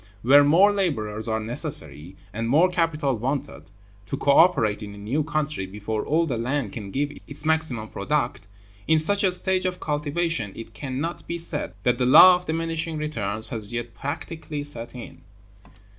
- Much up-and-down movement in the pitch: Yes, wide, 6.2 semitones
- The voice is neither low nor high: Yes, medium, 145 Hz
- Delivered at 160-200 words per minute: Yes, average, 175 wpm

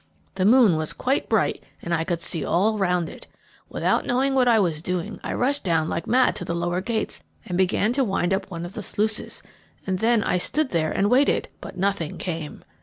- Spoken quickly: Yes, fast, 215 wpm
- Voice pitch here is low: No, high, 190 Hz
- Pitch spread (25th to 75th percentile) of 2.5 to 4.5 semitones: No, average, 5.1 semitones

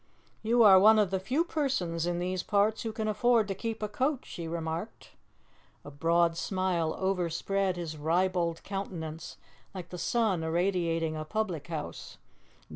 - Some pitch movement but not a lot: Yes, average, 4.1 semitones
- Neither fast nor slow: Yes, average, 155 wpm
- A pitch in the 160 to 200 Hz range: Yes, medium, 185 Hz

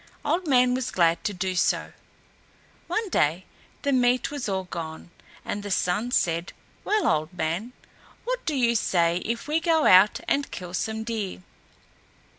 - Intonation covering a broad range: Yes, wide, 6.4 semitones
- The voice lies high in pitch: Yes, high, 215 Hz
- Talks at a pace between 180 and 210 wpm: No, average, 160 wpm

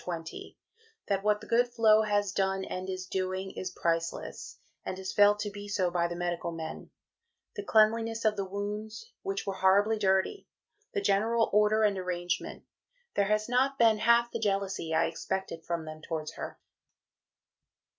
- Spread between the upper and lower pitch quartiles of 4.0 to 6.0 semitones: No, average, 2.9 semitones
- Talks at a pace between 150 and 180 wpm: Yes, average, 165 wpm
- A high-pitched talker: Yes, high, 200 Hz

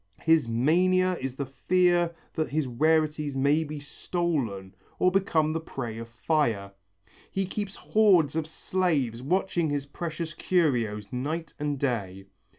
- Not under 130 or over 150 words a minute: Yes, average, 140 wpm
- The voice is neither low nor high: Yes, medium, 155 Hz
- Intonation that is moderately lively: Yes, average, 4.9 semitones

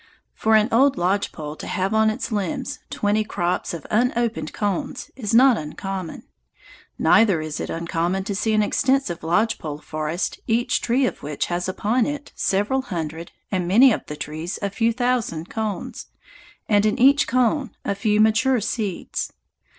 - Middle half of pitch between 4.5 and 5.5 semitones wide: Yes, average, 5.0 semitones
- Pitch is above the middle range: Yes, high, 210 Hz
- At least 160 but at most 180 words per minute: Yes, average, 165 wpm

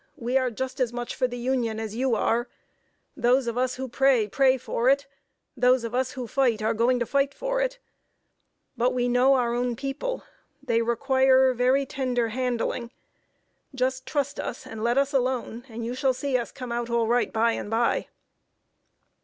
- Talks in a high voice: Yes, very high, 250 Hz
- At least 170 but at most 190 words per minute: Yes, average, 185 wpm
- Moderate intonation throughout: No, narrow, 1.9 semitones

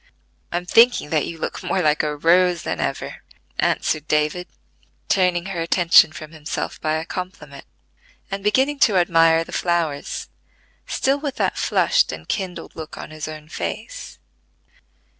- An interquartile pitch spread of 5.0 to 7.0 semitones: No, average, 3.1 semitones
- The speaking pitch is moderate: Yes, medium, 170 Hz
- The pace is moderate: Yes, average, 155 wpm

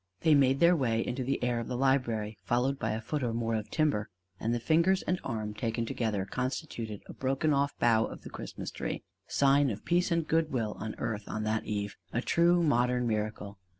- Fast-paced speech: Yes, fast, 215 wpm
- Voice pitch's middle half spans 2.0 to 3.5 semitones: No, average, 4.4 semitones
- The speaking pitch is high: No, low, 120 Hz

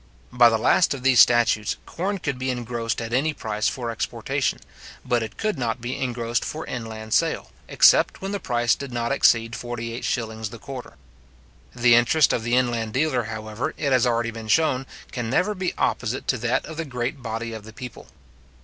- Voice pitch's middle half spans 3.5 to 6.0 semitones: No, narrow, 2.5 semitones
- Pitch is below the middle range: Yes, low, 120 Hz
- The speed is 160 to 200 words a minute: Yes, average, 190 wpm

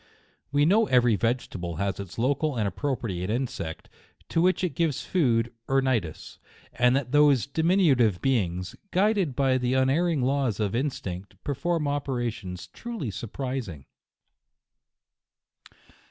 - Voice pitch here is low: Yes, low, 130 Hz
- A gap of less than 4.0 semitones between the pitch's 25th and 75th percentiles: No, wide, 5.5 semitones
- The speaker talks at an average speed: No, slow, 125 wpm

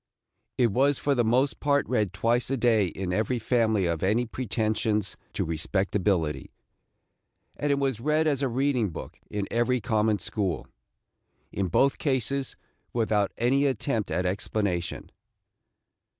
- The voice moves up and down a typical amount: Yes, average, 4.7 semitones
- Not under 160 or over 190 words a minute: No, average, 145 wpm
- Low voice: Yes, low, 115 Hz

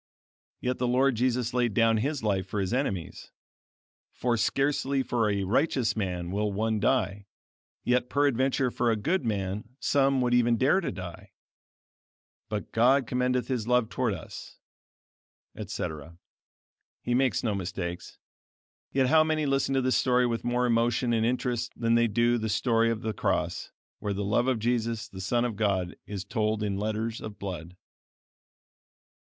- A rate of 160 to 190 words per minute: Yes, average, 165 wpm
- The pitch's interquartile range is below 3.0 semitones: No, average, 3.5 semitones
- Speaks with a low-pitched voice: Yes, low, 115 Hz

